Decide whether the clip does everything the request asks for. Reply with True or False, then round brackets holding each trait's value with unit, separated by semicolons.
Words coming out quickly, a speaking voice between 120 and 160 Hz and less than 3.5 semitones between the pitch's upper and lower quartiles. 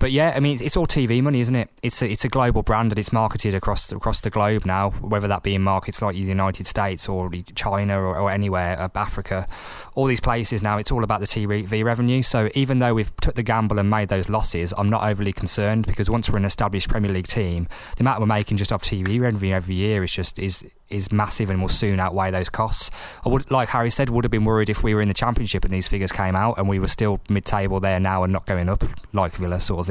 False (260 wpm; 105 Hz; 2.9 semitones)